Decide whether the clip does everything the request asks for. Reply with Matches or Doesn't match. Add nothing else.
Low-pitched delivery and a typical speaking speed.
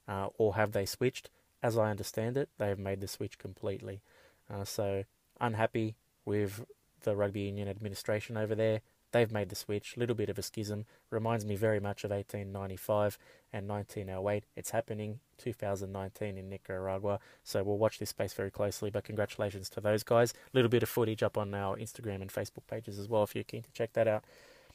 Matches